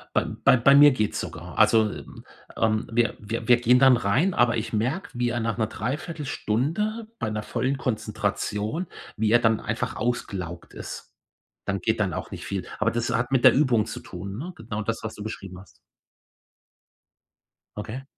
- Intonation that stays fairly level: No, average, 3.2 semitones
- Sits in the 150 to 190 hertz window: No, low, 115 Hz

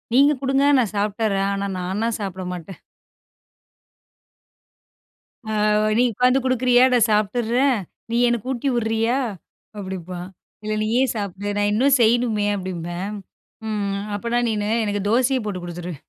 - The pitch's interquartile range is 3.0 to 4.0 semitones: Yes, average, 3.7 semitones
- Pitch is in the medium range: No, high, 215 Hz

